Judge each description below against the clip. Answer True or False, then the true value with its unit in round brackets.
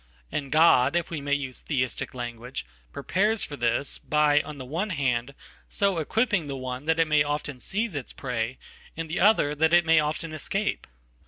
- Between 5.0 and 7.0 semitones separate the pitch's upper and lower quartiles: False (3.9 semitones)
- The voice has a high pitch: False (150 Hz)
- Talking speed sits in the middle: True (170 wpm)